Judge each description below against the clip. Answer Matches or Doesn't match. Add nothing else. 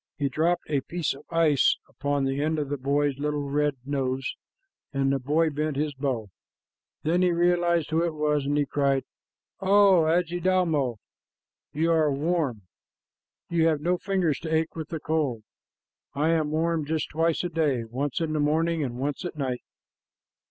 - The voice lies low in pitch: Doesn't match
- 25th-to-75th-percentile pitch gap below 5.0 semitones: Matches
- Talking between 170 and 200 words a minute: Matches